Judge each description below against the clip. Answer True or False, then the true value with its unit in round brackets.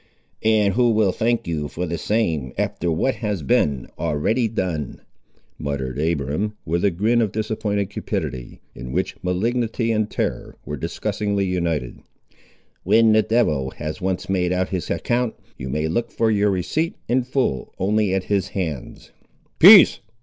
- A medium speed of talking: True (155 wpm)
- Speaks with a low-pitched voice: True (95 Hz)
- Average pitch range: False (5.8 semitones)